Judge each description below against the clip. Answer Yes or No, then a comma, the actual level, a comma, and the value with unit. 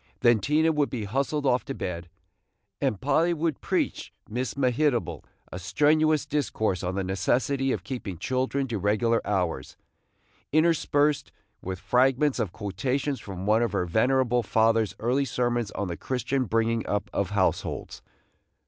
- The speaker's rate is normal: Yes, average, 150 wpm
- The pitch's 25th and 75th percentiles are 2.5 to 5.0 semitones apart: No, wide, 5.4 semitones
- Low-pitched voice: Yes, low, 120 Hz